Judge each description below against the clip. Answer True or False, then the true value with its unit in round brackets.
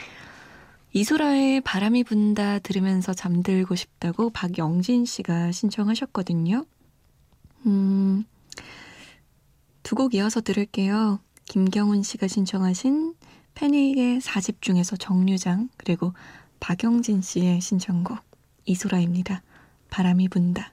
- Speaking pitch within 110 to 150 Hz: False (200 Hz)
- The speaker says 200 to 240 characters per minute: True (235 characters per minute)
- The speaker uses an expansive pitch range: False (3.4 semitones)